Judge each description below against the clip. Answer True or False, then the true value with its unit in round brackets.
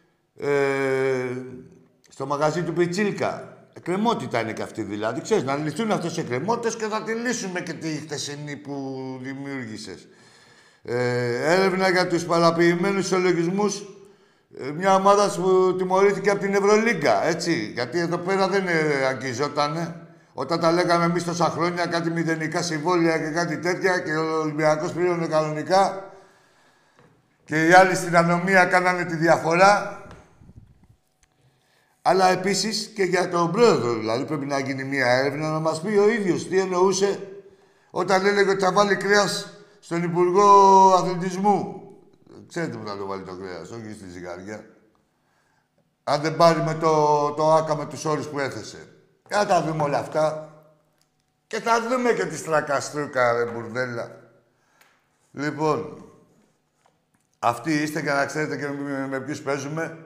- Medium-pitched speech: True (165 Hz)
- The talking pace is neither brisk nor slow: True (140 wpm)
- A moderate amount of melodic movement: True (4.8 semitones)